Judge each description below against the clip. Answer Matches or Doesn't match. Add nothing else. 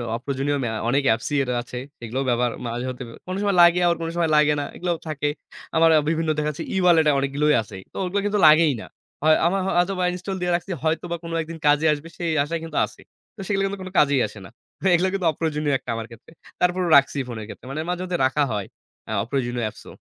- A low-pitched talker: Doesn't match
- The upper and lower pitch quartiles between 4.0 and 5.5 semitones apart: Matches